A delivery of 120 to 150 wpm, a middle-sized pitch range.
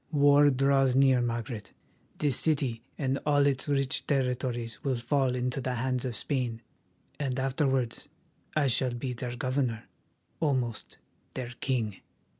No: slow, 135 wpm; narrow, 2.2 semitones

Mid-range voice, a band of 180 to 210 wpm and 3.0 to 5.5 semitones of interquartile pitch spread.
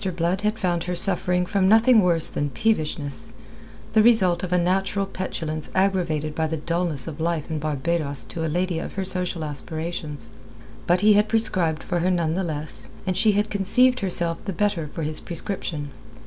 Yes: medium, 175 Hz; average, 185 wpm; average, 3.5 semitones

